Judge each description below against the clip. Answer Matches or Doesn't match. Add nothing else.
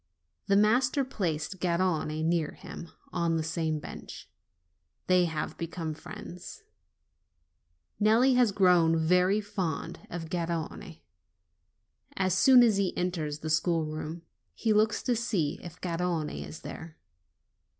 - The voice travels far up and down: Doesn't match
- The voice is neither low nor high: Matches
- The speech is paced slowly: Matches